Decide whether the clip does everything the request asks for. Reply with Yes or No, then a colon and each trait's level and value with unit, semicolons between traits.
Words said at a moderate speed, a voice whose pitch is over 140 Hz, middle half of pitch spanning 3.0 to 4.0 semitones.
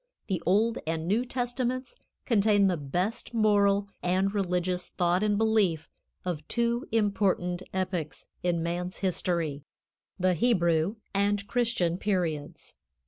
No: slow, 120 wpm; high, 190 Hz; average, 3.5 semitones